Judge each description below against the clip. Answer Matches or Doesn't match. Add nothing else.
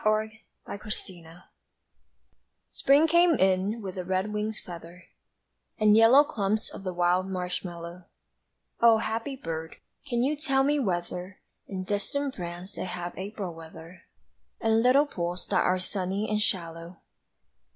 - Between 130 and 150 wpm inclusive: Matches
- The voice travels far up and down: Doesn't match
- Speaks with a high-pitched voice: Matches